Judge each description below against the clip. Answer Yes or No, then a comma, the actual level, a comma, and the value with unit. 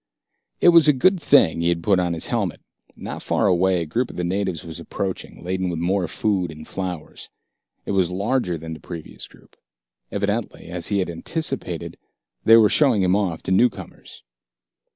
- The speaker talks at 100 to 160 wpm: No, average, 185 wpm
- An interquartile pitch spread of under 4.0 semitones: Yes, average, 3.5 semitones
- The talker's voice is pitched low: Yes, very low, 95 Hz